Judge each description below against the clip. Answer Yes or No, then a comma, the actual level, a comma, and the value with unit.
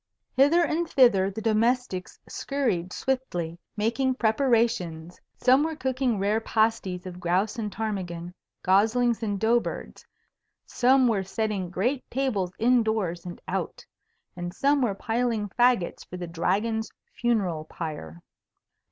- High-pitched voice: Yes, high, 220 Hz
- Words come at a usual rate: No, slow, 130 wpm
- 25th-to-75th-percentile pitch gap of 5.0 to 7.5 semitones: Yes, average, 5.3 semitones